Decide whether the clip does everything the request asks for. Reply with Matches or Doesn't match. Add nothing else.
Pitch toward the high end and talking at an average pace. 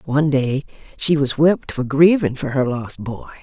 Doesn't match